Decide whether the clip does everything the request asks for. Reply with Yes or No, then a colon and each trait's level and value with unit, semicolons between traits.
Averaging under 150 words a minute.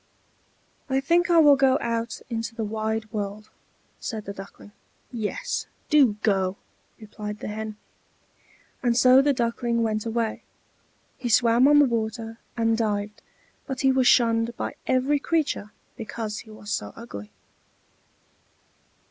Yes: average, 140 wpm